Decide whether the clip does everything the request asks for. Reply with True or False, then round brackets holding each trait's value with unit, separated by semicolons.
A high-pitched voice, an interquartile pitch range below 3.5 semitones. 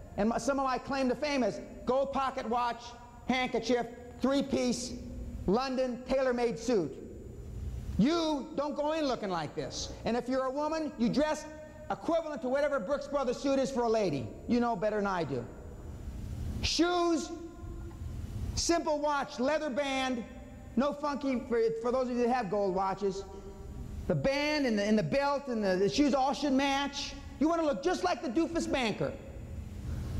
False (260 Hz; 3.9 semitones)